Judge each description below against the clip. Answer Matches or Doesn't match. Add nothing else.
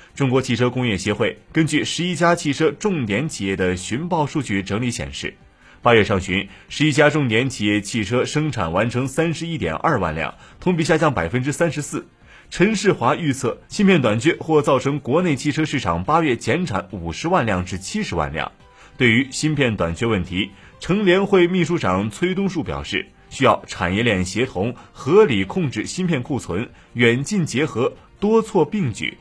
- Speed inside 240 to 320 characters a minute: Matches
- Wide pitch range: Matches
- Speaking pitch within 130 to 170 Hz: Matches